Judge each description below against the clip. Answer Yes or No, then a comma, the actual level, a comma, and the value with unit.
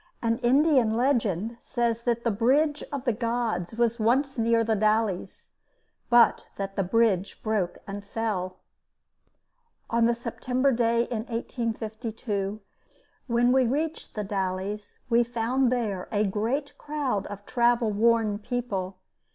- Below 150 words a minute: Yes, slow, 135 wpm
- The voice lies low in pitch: No, high, 230 Hz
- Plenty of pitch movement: No, average, 2.7 semitones